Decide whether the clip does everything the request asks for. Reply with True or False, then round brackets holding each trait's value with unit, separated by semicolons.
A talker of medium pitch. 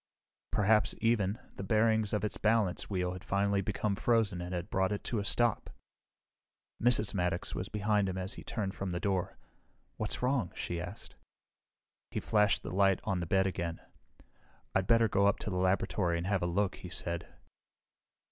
False (100 Hz)